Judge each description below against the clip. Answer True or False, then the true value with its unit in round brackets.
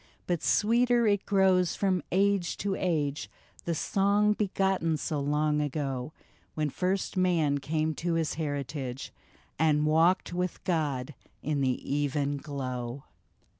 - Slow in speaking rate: True (130 wpm)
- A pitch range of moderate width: True (4.5 semitones)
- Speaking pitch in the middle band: True (160 Hz)